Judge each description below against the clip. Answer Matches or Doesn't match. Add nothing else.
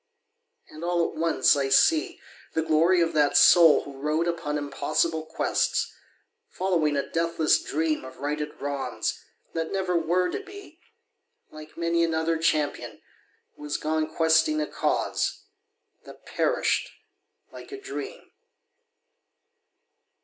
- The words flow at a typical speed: Doesn't match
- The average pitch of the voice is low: Doesn't match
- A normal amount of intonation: Doesn't match